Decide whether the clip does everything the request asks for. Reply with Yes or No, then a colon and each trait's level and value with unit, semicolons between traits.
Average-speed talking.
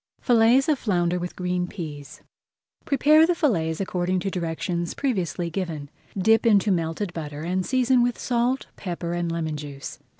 Yes: average, 155 wpm